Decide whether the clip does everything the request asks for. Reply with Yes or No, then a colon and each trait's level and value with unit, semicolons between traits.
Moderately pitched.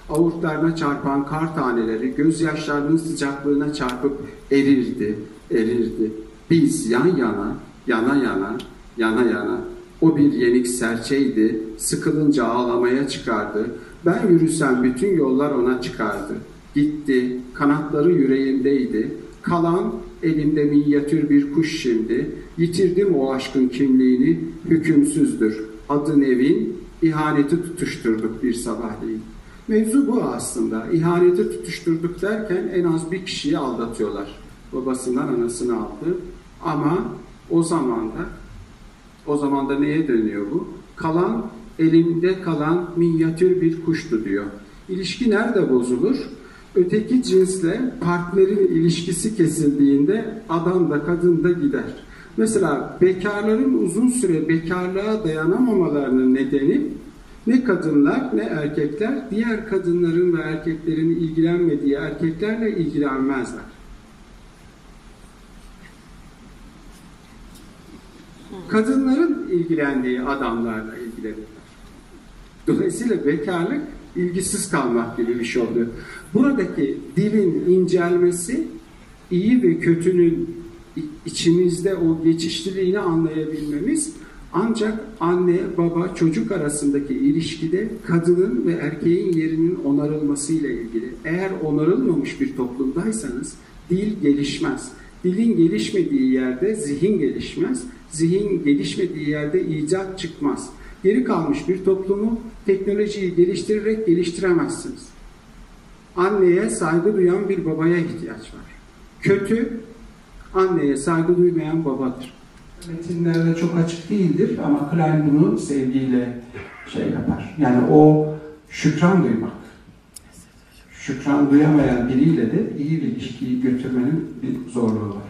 Yes: medium, 165 Hz